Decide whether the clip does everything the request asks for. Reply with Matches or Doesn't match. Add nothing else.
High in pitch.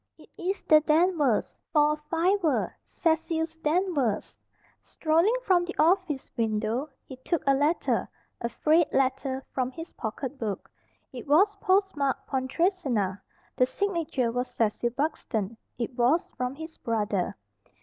Matches